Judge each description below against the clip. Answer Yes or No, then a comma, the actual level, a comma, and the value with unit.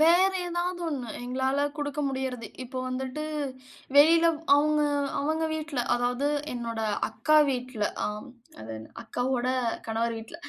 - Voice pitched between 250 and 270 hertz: Yes, very high, 265 Hz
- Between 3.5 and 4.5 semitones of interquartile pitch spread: Yes, average, 3.9 semitones